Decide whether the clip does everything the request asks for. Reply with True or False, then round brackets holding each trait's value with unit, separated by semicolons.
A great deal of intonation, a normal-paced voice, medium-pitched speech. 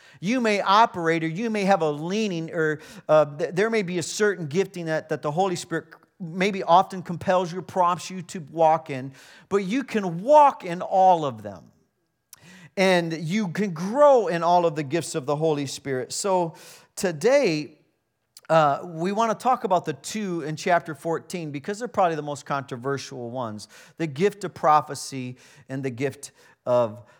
False (4.3 semitones; 175 wpm; 170 Hz)